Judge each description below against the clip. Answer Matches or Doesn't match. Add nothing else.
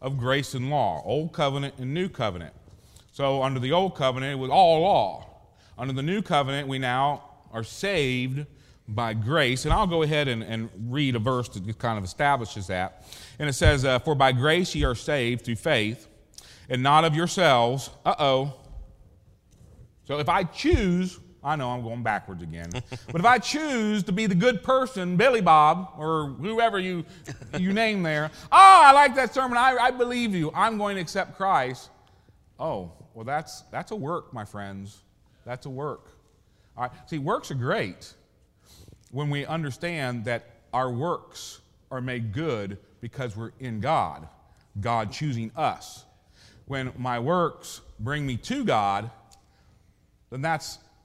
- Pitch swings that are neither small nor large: Doesn't match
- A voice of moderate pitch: Doesn't match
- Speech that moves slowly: Doesn't match